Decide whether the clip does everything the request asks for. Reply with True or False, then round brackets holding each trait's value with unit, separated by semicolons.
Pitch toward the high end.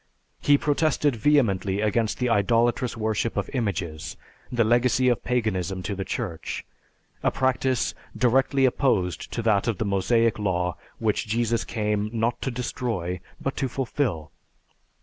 False (115 Hz)